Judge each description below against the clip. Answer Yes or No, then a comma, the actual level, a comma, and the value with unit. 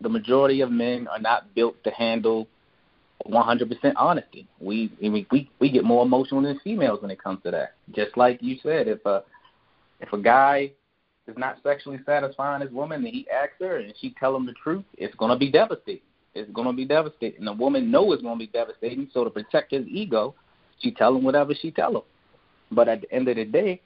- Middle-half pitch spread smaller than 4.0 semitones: No, average, 4.4 semitones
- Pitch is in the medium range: No, low, 130 Hz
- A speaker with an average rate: No, fast, 220 wpm